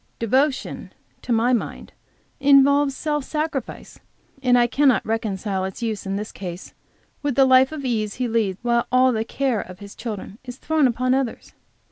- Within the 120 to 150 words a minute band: No, average, 170 wpm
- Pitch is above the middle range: Yes, high, 245 Hz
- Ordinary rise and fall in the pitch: Yes, average, 3.8 semitones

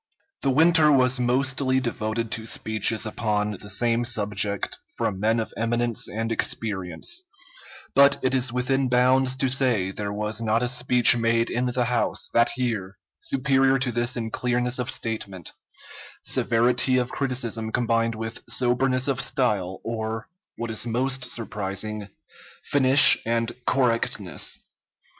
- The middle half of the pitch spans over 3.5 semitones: No, narrow, 2.5 semitones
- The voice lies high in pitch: No, low, 120 Hz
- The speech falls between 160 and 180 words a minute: No, average, 140 wpm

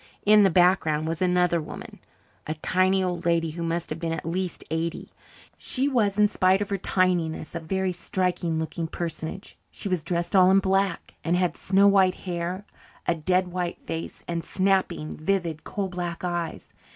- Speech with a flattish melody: Yes, narrow, 2.3 semitones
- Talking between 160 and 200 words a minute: Yes, average, 175 wpm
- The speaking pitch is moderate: Yes, medium, 180 Hz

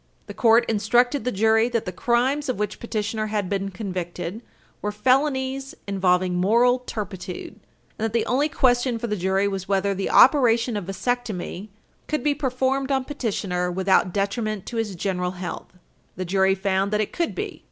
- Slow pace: No, average, 175 wpm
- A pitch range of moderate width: Yes, average, 4.3 semitones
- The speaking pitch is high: Yes, high, 215 Hz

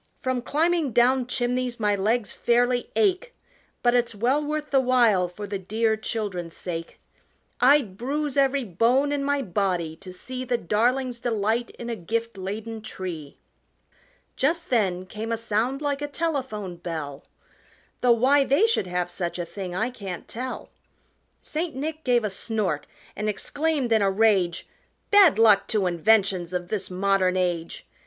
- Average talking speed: Yes, average, 160 wpm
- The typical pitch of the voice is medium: No, high, 225 Hz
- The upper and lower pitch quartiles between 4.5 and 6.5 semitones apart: Yes, wide, 5.4 semitones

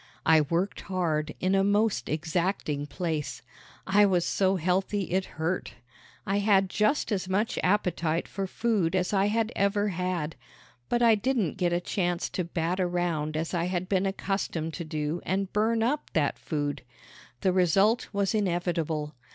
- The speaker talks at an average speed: Yes, average, 160 wpm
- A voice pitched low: No, medium, 185 Hz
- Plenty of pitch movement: No, average, 3.4 semitones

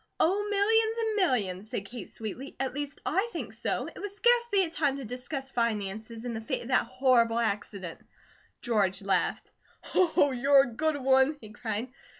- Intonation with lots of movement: Yes, wide, 6.4 semitones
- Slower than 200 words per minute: Yes, average, 175 wpm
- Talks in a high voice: Yes, very high, 260 Hz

